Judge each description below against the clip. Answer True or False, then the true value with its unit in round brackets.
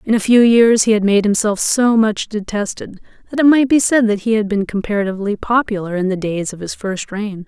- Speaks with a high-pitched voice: True (210 Hz)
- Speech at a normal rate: False (235 wpm)